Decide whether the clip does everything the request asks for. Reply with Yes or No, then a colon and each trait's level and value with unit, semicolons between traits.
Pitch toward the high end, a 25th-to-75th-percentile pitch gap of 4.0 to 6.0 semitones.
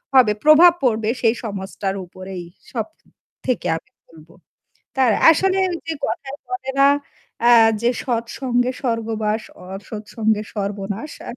Yes: high, 225 Hz; average, 4.5 semitones